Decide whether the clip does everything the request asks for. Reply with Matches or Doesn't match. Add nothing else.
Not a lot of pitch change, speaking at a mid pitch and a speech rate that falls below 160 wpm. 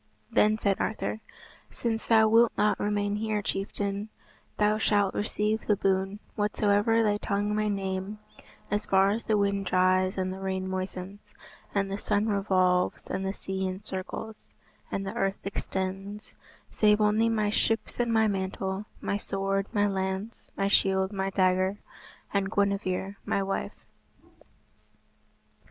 Doesn't match